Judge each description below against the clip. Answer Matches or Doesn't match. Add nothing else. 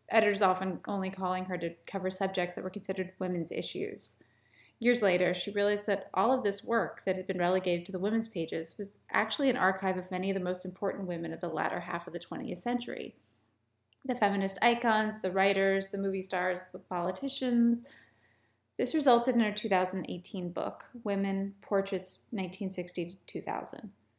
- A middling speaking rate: Matches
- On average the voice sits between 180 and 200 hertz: Matches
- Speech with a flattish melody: Matches